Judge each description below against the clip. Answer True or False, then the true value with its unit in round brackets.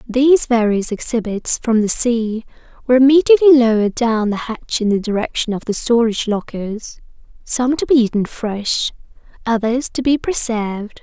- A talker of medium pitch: False (235 Hz)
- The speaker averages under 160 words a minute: True (150 wpm)